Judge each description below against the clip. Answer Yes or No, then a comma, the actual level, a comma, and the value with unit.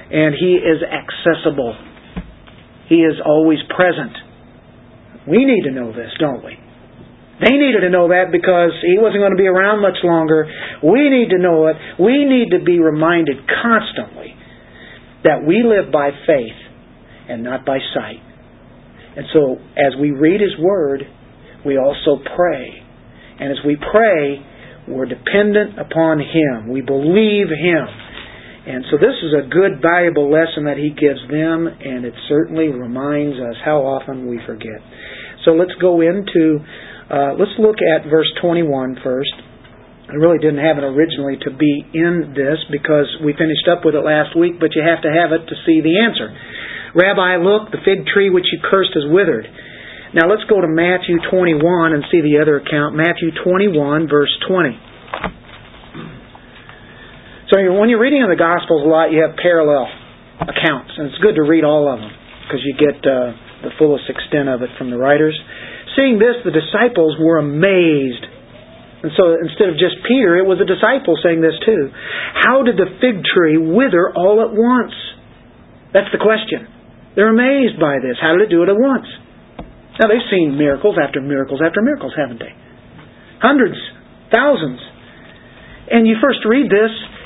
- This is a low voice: No, medium, 160 Hz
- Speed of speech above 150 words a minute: Yes, average, 170 wpm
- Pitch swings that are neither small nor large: Yes, average, 4.5 semitones